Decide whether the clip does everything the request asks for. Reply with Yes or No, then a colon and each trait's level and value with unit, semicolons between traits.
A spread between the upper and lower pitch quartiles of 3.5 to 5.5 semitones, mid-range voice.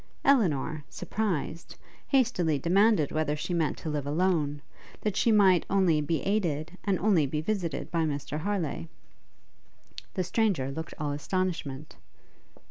Yes: average, 4.6 semitones; medium, 165 Hz